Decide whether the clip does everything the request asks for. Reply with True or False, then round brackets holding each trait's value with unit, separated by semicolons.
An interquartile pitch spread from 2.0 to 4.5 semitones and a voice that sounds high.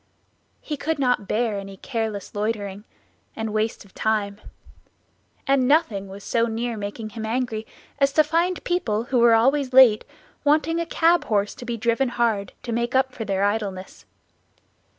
True (4.2 semitones; 230 Hz)